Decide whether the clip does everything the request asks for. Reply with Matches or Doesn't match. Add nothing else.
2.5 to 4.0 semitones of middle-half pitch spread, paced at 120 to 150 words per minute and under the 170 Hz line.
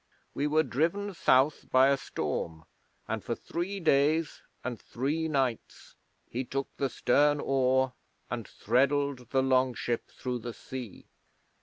Matches